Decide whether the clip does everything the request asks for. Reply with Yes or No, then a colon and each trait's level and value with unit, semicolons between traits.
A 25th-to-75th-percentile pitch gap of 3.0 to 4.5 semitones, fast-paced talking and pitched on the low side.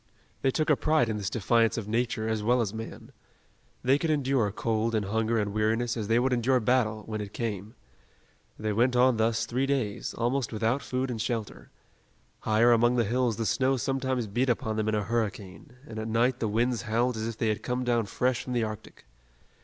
No: narrow, 2.4 semitones; fast, 210 wpm; low, 115 Hz